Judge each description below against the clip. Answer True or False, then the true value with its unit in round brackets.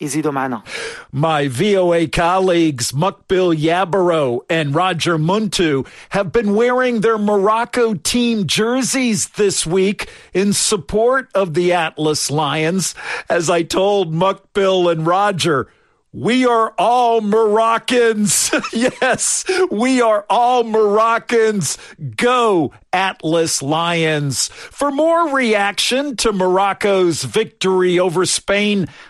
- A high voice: True (195 Hz)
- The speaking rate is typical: False (100 wpm)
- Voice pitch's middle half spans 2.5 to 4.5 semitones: False (5.0 semitones)